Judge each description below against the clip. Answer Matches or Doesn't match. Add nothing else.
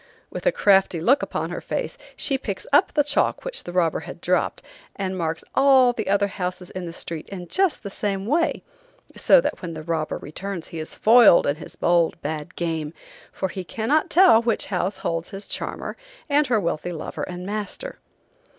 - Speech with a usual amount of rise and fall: Doesn't match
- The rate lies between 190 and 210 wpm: Matches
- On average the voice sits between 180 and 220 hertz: Matches